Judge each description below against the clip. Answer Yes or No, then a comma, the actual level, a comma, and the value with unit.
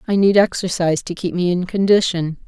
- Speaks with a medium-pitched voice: Yes, medium, 180 Hz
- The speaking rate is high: No, average, 195 wpm